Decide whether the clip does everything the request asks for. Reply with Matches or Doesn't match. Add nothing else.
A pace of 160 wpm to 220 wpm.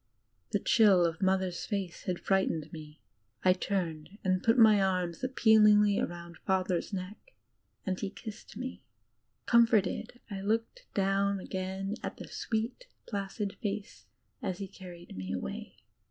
Doesn't match